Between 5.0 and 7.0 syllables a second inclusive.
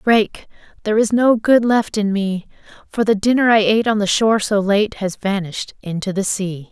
Yes: 5.2 syllables/s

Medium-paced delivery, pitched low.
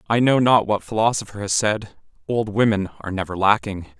Yes: average, 180 wpm; low, 105 Hz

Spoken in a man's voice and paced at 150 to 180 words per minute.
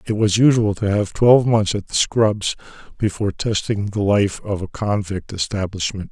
Yes: male; average, 175 wpm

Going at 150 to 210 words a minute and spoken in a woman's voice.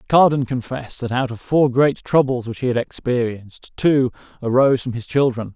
No: average, 185 wpm; male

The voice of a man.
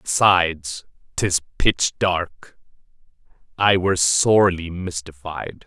Yes: male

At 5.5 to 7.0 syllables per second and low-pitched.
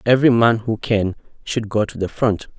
No: 5.1 syllables/s; low, 110 Hz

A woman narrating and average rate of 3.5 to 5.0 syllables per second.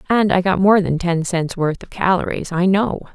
Yes: female; 4.9 syllables/s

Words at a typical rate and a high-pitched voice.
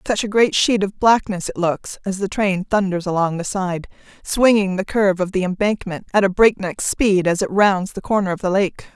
No: fast, 220 wpm; high, 195 Hz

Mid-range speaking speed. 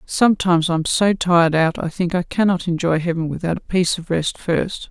No: fast, 210 wpm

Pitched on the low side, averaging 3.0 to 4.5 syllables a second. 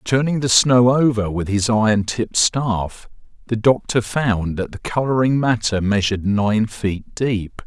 Yes: low, 115 Hz; 4.2 syllables/s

